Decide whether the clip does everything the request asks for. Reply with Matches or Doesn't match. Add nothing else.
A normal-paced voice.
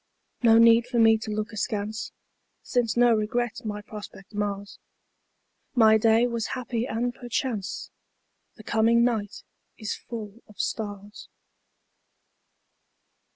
Doesn't match